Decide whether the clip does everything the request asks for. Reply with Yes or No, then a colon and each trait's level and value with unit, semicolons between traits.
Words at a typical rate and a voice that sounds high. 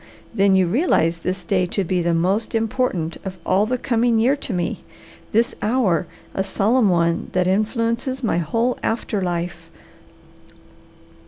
Yes: average, 150 wpm; high, 195 Hz